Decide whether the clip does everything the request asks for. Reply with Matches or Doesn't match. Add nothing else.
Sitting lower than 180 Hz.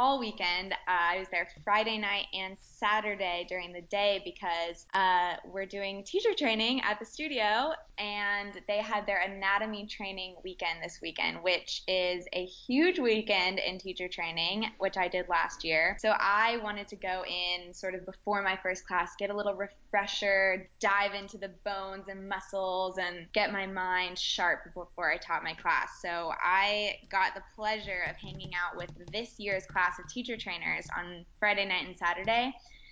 Doesn't match